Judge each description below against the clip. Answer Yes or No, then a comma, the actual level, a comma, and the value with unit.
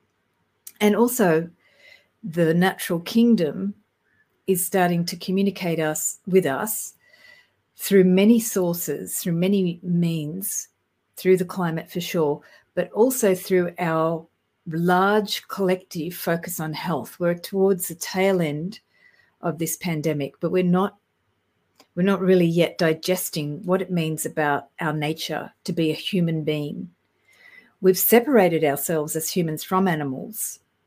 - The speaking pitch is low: No, medium, 180 Hz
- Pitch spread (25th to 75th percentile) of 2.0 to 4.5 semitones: Yes, average, 3.0 semitones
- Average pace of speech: No, slow, 130 wpm